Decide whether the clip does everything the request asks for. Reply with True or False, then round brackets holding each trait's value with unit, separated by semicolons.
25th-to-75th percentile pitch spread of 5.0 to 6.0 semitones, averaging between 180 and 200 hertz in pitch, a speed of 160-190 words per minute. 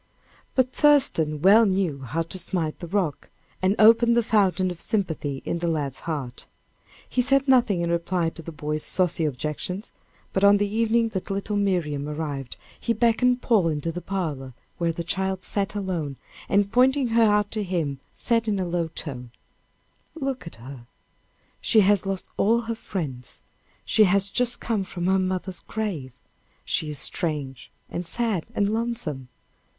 True (5.6 semitones; 185 Hz; 165 wpm)